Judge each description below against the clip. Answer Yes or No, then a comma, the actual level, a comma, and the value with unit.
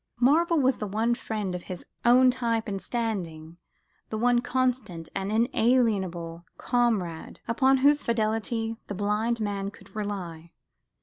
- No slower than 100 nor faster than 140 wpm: Yes, slow, 135 wpm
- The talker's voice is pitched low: No, high, 220 Hz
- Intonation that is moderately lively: Yes, average, 4.0 semitones